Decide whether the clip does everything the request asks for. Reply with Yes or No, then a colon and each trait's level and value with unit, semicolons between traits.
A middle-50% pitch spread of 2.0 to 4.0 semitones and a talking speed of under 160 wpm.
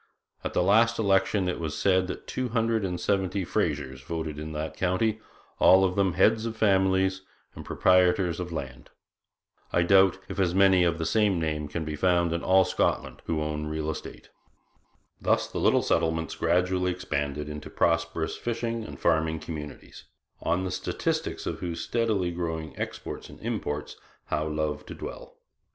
No: average, 3.4 semitones; average, 170 wpm